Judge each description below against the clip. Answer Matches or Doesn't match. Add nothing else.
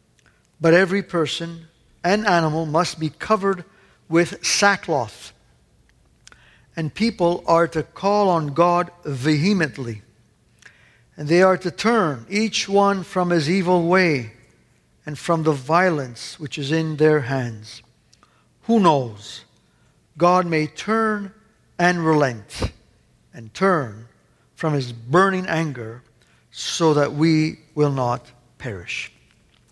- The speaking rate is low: Matches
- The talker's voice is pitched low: Doesn't match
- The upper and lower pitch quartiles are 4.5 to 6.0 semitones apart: Matches